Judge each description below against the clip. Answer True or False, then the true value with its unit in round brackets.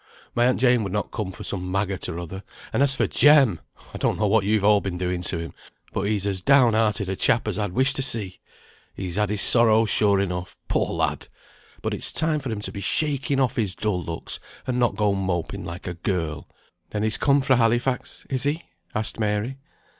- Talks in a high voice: False (105 Hz)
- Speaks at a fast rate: True (220 wpm)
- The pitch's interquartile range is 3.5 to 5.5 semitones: True (4.6 semitones)